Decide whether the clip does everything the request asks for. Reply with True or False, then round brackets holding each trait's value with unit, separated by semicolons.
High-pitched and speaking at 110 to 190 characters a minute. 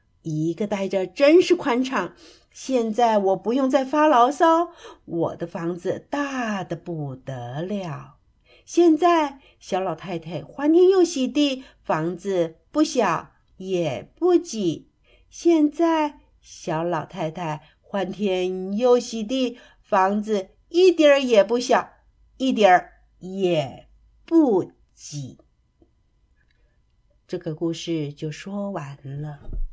True (195 Hz; 155 characters per minute)